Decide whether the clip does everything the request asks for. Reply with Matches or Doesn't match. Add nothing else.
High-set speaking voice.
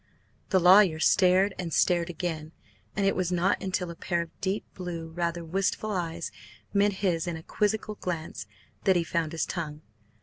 Doesn't match